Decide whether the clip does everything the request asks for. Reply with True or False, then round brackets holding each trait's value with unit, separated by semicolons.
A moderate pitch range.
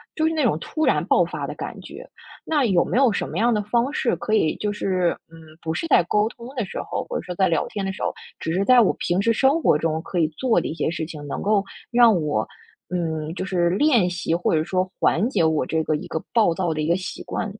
False (5.9 semitones)